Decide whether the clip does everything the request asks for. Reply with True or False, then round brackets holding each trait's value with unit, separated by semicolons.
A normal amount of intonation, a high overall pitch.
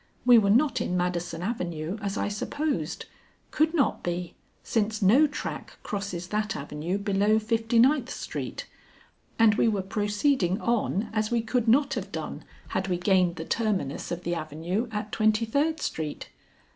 True (4.4 semitones; 210 Hz)